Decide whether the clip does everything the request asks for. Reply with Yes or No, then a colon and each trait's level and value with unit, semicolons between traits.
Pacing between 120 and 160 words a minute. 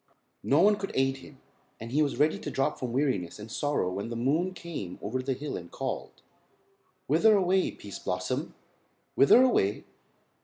No: average, 175 wpm